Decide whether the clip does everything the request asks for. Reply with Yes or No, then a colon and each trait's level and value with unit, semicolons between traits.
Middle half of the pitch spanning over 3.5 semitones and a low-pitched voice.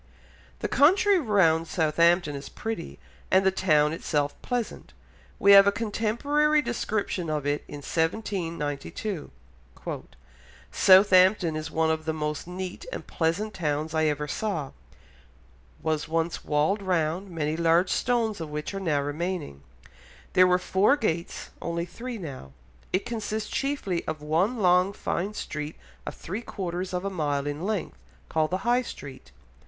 No: average, 4.7 semitones; medium, 175 Hz